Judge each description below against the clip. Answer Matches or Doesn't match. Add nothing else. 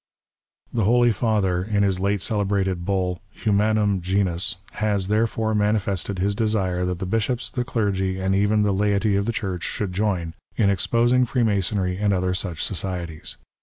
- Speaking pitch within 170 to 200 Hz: Doesn't match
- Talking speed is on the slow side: Doesn't match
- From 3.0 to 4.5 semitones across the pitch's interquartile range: Doesn't match